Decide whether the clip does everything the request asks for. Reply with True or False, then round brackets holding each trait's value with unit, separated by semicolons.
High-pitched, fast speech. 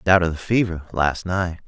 False (90 Hz; 215 wpm)